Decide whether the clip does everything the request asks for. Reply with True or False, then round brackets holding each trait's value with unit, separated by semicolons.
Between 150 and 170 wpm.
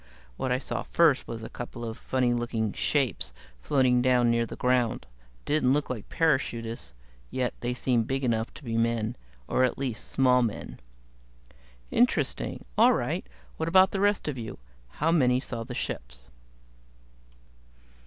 True (155 wpm)